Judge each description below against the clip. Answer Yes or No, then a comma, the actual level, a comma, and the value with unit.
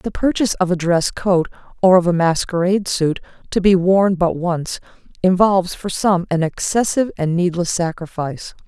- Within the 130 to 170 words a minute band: Yes, average, 165 wpm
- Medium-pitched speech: Yes, medium, 180 Hz